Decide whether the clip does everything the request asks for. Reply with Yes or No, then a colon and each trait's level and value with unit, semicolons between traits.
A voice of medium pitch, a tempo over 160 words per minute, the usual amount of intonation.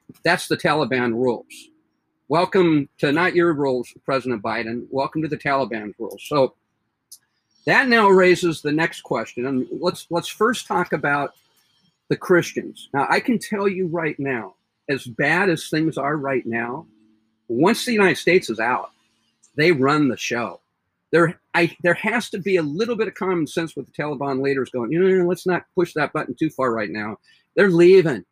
No: medium, 155 Hz; average, 180 wpm; wide, 5.8 semitones